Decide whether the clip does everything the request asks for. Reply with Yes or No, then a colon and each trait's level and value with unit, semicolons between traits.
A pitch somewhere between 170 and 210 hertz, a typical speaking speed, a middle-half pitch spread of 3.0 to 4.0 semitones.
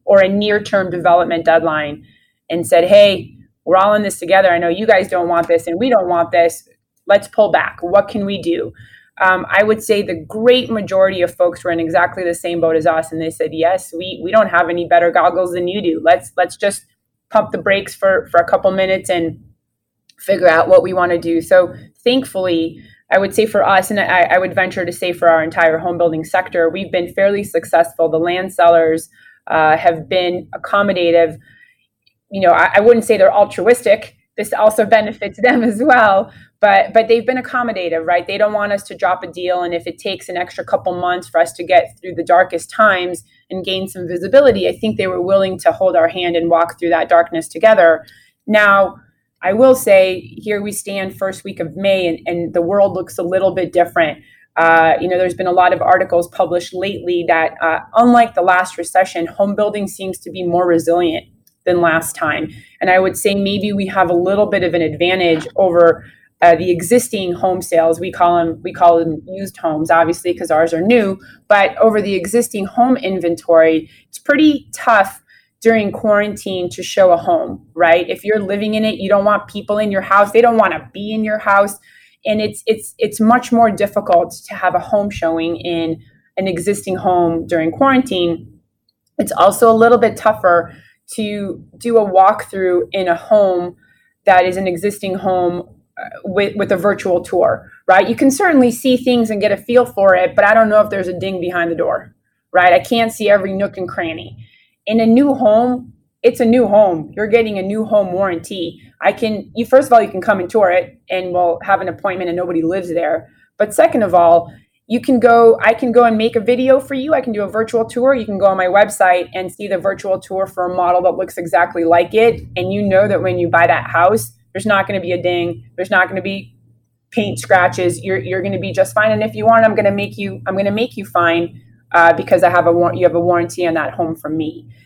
No: medium, 185 Hz; fast, 220 wpm; average, 3.4 semitones